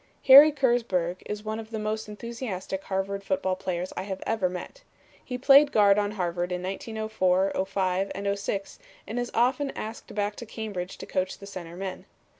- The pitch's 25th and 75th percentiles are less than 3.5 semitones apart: Yes, average, 3.0 semitones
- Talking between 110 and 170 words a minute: No, average, 180 wpm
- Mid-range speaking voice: No, high, 200 Hz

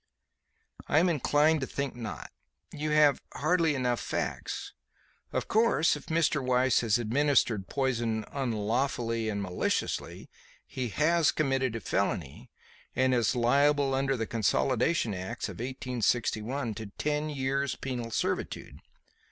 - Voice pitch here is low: Yes, low, 130 Hz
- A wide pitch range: No, average, 4.1 semitones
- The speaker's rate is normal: No, slow, 125 wpm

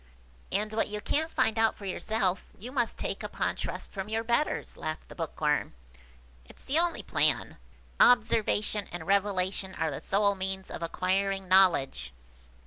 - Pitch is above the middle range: Yes, high, 200 Hz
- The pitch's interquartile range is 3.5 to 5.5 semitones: No, average, 3.1 semitones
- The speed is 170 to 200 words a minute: No, average, 155 wpm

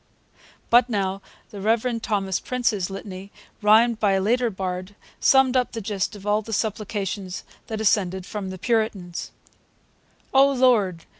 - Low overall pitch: No, high, 210 Hz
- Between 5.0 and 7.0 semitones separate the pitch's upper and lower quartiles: No, average, 3.2 semitones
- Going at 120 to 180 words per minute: Yes, average, 145 wpm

